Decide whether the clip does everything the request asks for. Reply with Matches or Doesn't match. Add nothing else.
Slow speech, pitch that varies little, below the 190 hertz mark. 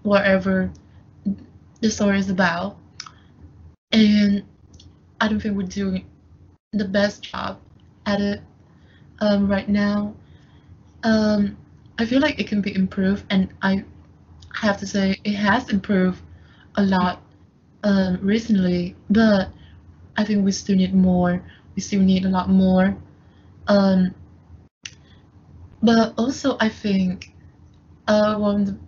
Doesn't match